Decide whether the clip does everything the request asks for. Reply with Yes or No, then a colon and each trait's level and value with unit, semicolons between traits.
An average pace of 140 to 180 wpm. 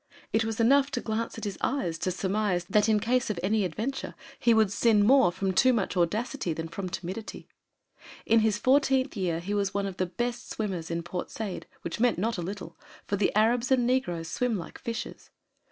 No: fast, 205 wpm